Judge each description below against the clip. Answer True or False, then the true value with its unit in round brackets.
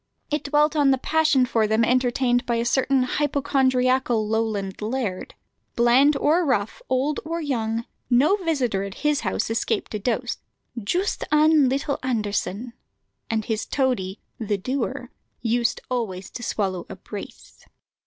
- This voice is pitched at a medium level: False (250 Hz)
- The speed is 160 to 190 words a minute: False (145 wpm)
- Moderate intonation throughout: True (4.1 semitones)